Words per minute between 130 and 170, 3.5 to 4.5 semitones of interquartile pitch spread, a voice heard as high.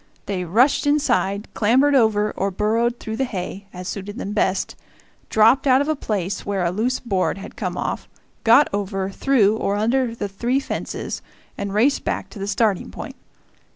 No: average, 180 wpm; average, 3.9 semitones; high, 215 Hz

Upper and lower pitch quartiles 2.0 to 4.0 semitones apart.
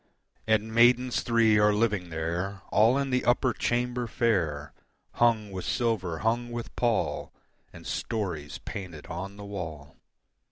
No: average, 4.9 semitones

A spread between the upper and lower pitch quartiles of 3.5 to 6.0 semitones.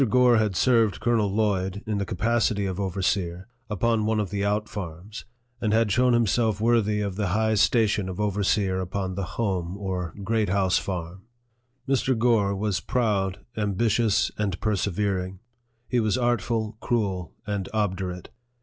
No: narrow, 2.6 semitones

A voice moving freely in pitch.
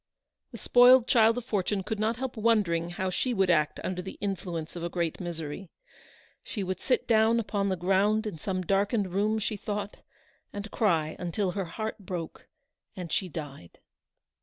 No: average, 3.8 semitones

